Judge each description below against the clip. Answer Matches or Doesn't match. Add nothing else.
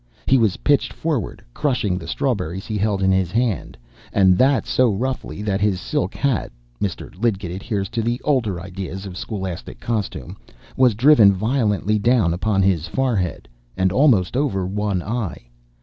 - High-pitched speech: Doesn't match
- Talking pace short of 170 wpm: Matches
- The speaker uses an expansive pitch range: Doesn't match